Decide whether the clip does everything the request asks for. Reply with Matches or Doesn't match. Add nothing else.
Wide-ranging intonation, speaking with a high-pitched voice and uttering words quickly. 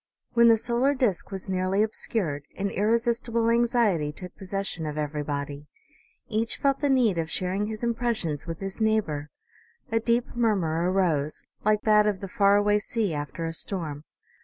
Doesn't match